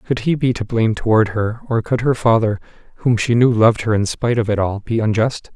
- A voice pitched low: Yes, low, 115 Hz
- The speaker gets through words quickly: Yes, fast, 250 wpm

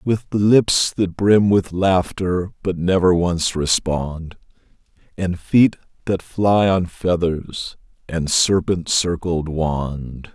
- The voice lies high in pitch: No, very low, 90 Hz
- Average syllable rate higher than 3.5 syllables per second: No, 3.0 syllables/s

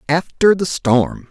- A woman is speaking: No, male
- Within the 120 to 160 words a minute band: Yes, average, 140 wpm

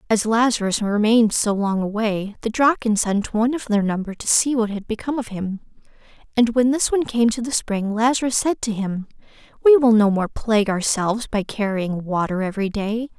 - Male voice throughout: No, female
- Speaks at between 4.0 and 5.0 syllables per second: No, 5.5 syllables/s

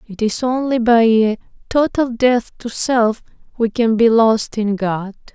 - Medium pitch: No, high, 230 Hz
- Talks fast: No, average, 170 wpm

